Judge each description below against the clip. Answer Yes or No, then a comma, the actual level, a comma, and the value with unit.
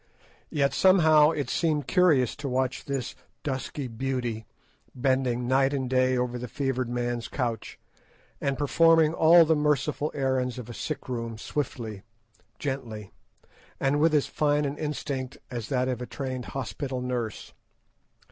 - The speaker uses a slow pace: No, average, 145 wpm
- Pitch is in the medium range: No, low, 130 Hz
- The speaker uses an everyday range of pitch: Yes, average, 3.0 semitones